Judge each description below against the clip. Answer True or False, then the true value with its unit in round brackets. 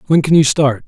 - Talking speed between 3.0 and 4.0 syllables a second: False (5.6 syllables/s)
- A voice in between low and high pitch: True (145 Hz)